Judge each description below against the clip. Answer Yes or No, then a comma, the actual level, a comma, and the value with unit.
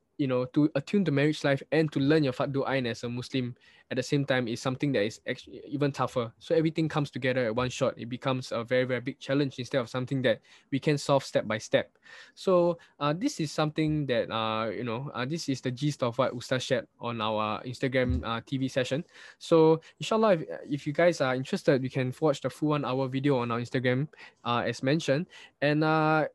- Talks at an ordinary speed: No, fast, 225 wpm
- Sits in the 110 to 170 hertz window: Yes, low, 135 Hz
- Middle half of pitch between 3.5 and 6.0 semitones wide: No, average, 3.0 semitones